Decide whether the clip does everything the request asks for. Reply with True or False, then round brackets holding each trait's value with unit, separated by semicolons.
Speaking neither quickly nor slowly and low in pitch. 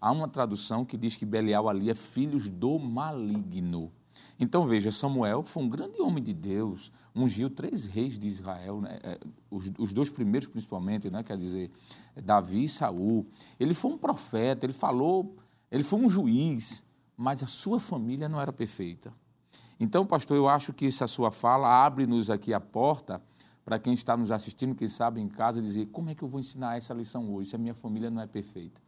False (195 wpm; 115 Hz)